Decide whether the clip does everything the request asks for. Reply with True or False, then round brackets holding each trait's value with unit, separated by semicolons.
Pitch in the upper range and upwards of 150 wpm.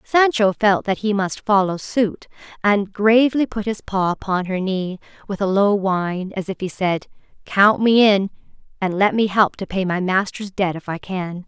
True (195 Hz; 200 wpm)